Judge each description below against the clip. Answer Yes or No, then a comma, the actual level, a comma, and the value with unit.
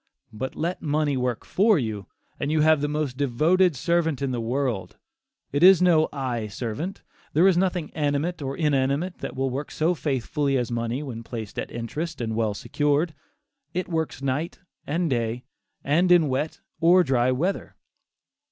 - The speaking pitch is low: No, medium, 145 Hz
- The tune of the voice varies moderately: Yes, average, 4.7 semitones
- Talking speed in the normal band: Yes, average, 165 wpm